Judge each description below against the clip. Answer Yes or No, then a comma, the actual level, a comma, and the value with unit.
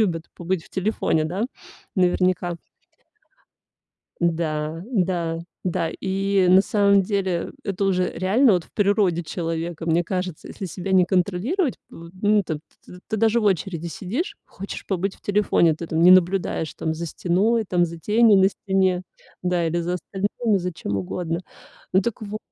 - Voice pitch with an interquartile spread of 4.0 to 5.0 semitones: No, average, 2.8 semitones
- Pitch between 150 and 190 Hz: Yes, medium, 185 Hz